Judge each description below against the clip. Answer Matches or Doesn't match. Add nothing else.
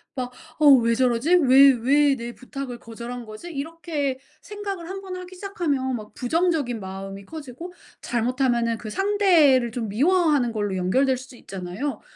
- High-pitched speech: Matches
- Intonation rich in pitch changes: Matches